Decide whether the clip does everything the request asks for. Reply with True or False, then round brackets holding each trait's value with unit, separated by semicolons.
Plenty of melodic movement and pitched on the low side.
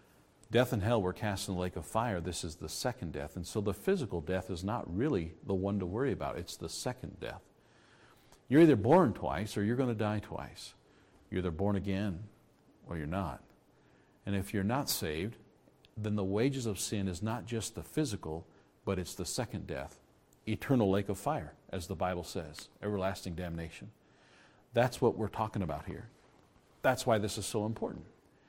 False (3.5 semitones; 100 Hz)